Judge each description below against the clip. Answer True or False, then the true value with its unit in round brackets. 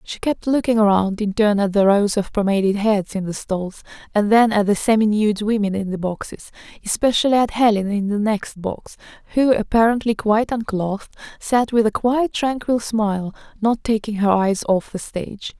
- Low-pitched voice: False (215 Hz)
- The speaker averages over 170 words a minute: True (180 wpm)